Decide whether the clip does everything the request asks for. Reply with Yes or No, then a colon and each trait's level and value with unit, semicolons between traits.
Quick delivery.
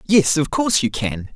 Yes: fast, 220 wpm